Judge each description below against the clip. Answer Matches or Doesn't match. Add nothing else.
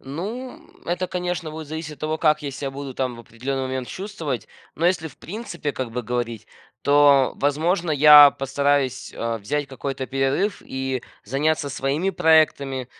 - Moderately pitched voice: Matches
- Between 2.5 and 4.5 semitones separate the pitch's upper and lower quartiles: Matches